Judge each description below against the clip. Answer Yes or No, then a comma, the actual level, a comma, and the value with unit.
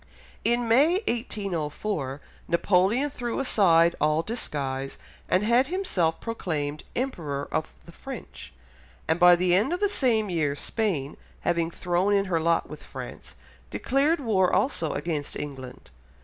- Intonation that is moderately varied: No, wide, 7.0 semitones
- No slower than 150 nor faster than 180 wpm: No, slow, 135 wpm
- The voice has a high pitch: No, medium, 180 Hz